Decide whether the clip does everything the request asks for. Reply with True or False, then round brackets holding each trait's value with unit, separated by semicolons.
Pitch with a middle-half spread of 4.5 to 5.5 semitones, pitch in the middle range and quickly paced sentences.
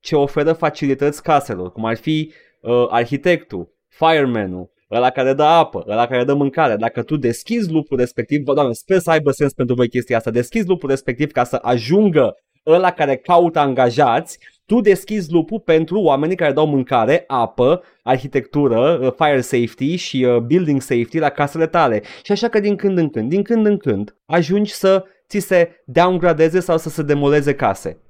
True (5.2 semitones; 145 Hz; 180 wpm)